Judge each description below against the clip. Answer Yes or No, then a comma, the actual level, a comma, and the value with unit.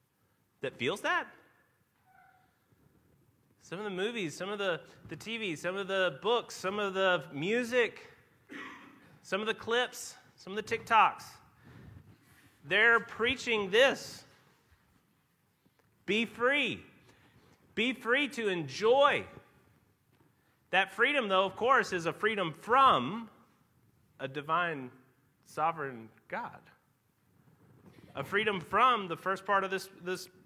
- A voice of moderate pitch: No, high, 195 Hz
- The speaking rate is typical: No, slow, 115 wpm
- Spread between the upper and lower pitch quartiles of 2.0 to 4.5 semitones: No, average, 5.2 semitones